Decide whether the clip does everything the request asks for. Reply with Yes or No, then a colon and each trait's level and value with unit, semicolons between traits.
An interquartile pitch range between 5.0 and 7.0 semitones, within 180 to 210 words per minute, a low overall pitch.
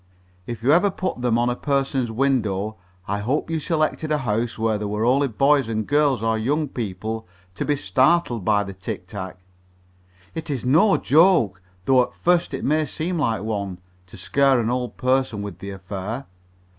Yes: average, 5.3 semitones; average, 185 wpm; low, 120 Hz